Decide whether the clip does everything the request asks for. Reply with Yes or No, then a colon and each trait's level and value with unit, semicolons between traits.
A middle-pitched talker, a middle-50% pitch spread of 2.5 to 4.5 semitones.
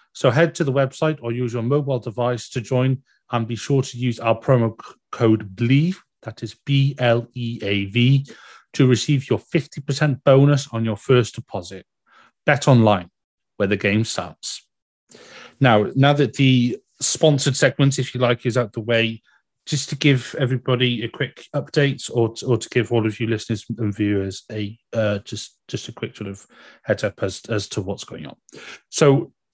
No: low, 125 Hz; average, 3.3 semitones